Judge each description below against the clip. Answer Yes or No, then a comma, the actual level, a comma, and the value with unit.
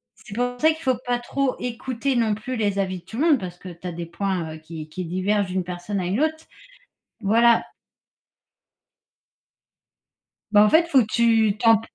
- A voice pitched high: Yes, high, 215 Hz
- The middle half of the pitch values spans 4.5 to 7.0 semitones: Yes, average, 5.0 semitones